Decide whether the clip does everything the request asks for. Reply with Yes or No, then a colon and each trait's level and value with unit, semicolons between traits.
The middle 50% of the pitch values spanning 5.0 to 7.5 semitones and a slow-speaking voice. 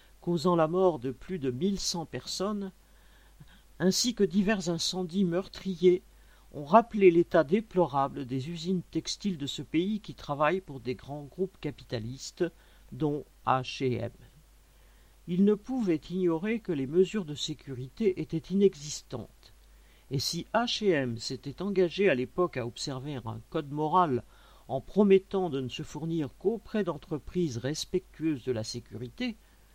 Yes: wide, 5.6 semitones; slow, 135 wpm